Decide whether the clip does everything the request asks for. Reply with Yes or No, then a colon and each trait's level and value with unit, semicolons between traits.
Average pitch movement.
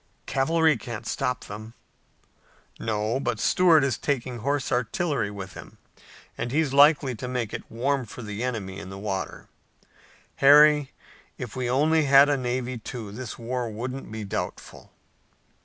Yes: average, 4.1 semitones